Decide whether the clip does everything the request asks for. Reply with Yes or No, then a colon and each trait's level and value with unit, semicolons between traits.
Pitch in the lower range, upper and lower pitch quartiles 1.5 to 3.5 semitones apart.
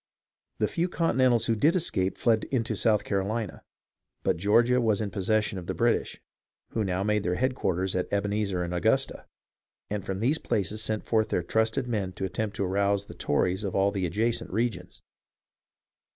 Yes: low, 105 Hz; average, 3.1 semitones